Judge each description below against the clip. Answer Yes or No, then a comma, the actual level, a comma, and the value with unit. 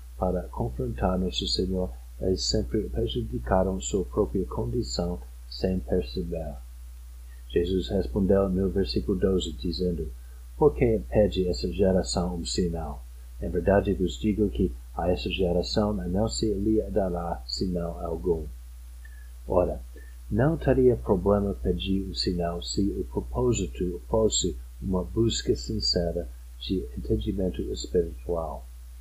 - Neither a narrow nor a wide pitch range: No, wide, 7.6 semitones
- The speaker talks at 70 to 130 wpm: Yes, slow, 120 wpm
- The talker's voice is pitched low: Yes, very low, 90 Hz